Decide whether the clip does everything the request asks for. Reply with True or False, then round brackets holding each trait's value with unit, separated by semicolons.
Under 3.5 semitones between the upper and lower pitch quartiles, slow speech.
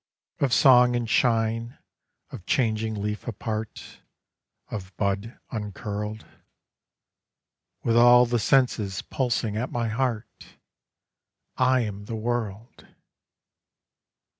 True (2.4 semitones; 95 wpm)